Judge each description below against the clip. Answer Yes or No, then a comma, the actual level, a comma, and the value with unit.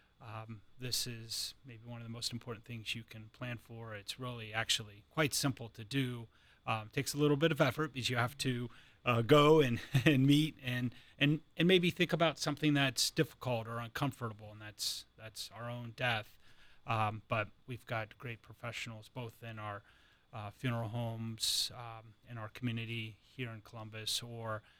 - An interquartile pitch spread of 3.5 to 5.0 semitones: No, average, 2.8 semitones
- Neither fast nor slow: Yes, average, 180 wpm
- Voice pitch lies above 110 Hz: Yes, low, 120 Hz